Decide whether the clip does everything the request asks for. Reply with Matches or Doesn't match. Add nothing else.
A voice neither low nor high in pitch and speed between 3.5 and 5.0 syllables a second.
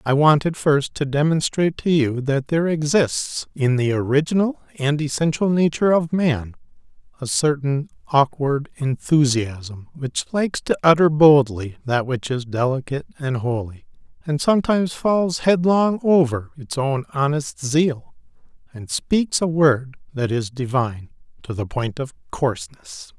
Matches